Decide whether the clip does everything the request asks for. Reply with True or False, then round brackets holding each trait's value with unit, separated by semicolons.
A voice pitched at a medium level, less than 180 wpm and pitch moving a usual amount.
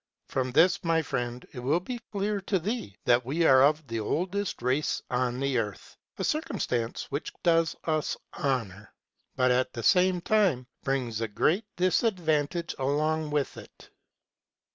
False (150 Hz; 155 wpm; 5.8 semitones)